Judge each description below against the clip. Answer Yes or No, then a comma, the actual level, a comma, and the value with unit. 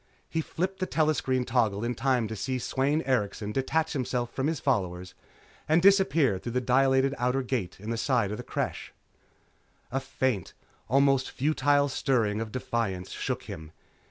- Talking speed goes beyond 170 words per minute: No, average, 160 wpm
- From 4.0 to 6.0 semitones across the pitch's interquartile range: No, average, 3.6 semitones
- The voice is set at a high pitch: No, low, 130 Hz